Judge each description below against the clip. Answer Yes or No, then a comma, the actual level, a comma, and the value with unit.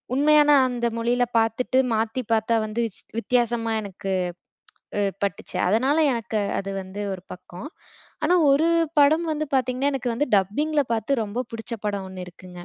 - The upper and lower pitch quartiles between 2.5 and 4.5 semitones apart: No, average, 4.9 semitones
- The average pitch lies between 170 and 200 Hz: No, high, 230 Hz